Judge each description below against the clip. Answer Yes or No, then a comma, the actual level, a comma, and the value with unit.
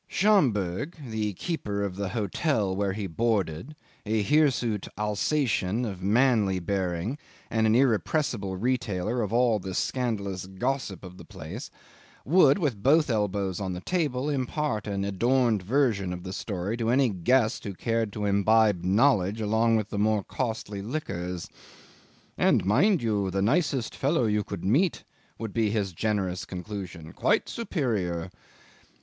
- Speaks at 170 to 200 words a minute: No, average, 145 wpm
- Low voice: Yes, low, 105 Hz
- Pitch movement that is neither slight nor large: Yes, average, 4.5 semitones